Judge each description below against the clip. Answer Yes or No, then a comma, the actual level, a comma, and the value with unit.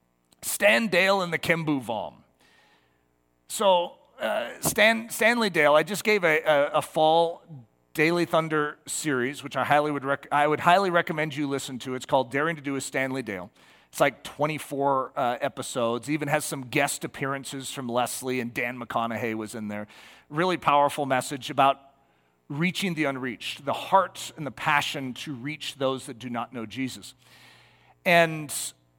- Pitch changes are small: No, average, 3.7 semitones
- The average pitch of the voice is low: No, medium, 145 Hz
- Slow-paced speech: No, average, 165 wpm